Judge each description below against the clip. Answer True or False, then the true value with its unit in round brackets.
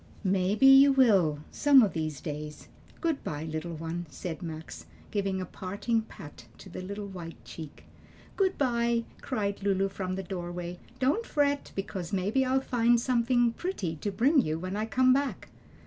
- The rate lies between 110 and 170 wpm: True (165 wpm)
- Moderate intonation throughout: False (6.6 semitones)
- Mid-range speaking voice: False (200 Hz)